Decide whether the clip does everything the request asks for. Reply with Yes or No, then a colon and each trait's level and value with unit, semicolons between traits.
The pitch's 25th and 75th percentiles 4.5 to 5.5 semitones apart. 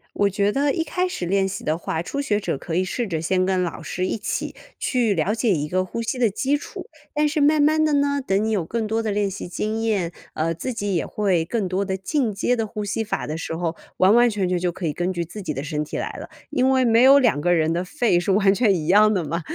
Yes: average, 4.9 semitones